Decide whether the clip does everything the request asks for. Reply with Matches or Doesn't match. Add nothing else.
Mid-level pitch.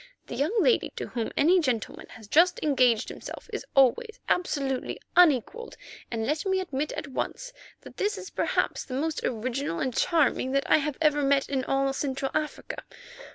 Doesn't match